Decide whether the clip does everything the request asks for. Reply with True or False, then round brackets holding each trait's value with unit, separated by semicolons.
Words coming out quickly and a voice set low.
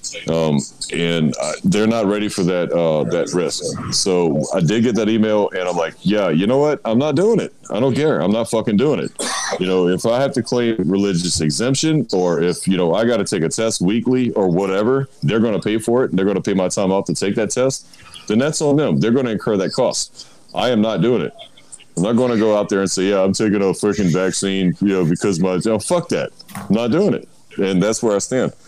True (255 wpm; 105 Hz)